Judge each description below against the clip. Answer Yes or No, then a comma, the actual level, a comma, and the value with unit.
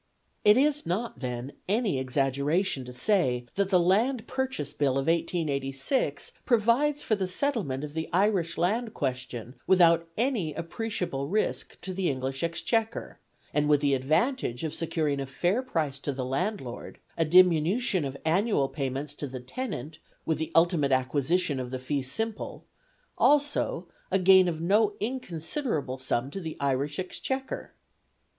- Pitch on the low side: No, medium, 165 Hz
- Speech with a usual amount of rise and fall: No, wide, 7.2 semitones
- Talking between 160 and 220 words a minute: No, average, 150 wpm